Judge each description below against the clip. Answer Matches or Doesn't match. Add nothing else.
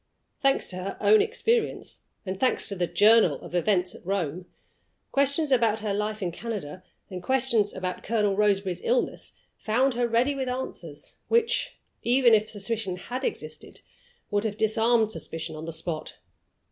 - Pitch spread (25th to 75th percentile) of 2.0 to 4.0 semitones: Doesn't match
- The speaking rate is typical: Matches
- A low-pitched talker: Doesn't match